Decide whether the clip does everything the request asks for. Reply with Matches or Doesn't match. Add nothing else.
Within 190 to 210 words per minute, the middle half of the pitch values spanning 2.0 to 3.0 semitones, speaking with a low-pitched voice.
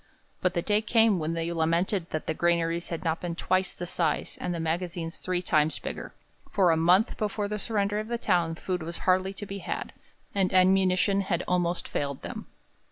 Doesn't match